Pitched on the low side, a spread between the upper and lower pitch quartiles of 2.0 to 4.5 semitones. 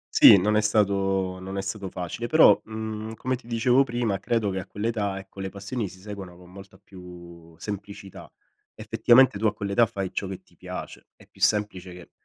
Yes: low, 100 Hz; narrow, 2.6 semitones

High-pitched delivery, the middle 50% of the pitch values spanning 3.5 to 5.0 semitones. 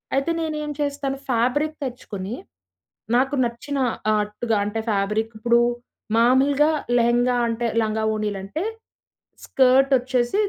Yes: high, 245 Hz; average, 3.8 semitones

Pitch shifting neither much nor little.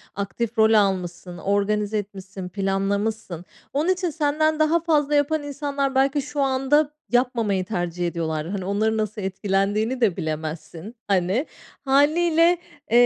No: wide, 6.8 semitones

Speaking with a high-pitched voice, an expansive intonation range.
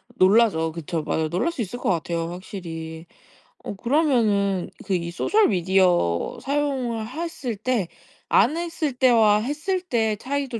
Yes: high, 215 Hz; wide, 7.3 semitones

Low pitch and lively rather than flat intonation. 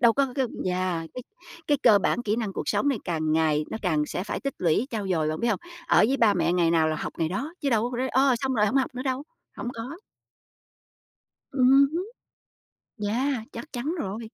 No: high, 225 Hz; wide, 6.4 semitones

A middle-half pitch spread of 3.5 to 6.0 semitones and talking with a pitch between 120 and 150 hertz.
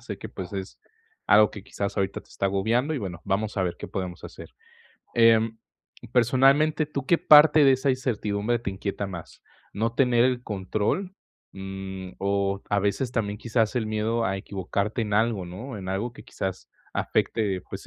No: average, 4.0 semitones; low, 105 Hz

